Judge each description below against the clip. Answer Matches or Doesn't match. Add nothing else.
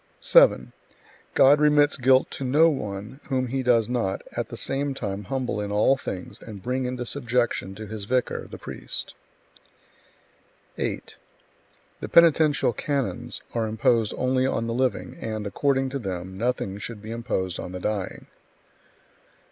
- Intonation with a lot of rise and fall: Doesn't match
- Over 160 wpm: Doesn't match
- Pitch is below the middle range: Matches